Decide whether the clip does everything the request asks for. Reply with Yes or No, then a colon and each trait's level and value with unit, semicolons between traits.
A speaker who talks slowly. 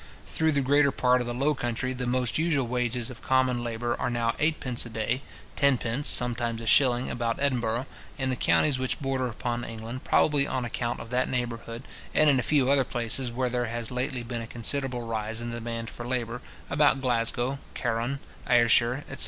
No: average, 200 wpm